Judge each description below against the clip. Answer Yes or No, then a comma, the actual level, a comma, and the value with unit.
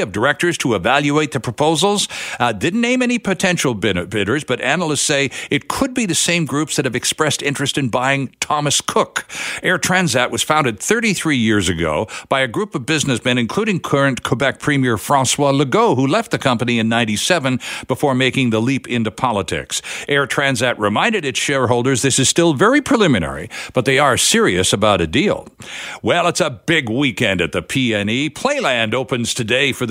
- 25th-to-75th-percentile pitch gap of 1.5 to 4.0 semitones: No, average, 4.4 semitones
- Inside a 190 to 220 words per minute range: No, average, 180 wpm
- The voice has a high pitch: No, medium, 140 Hz